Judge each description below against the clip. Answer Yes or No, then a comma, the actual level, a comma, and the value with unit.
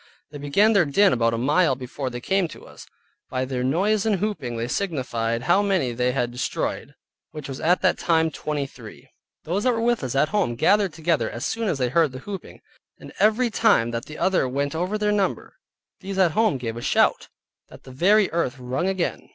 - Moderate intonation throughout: No, wide, 7.6 semitones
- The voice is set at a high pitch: No, medium, 155 Hz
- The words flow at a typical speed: No, fast, 215 wpm